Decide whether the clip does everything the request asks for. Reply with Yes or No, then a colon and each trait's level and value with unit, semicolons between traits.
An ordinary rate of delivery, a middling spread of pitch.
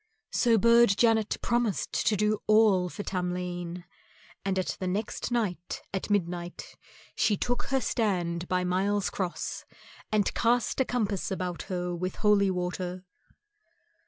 No: slow, 130 wpm; average, 3.3 semitones